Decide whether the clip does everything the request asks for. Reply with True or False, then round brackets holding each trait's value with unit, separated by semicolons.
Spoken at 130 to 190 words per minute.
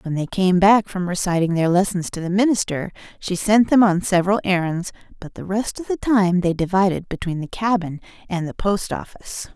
False (200 wpm)